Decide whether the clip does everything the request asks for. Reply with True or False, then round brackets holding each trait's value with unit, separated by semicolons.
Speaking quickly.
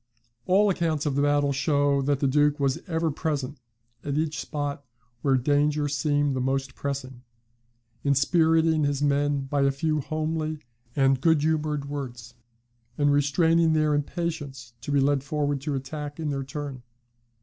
False (160 wpm)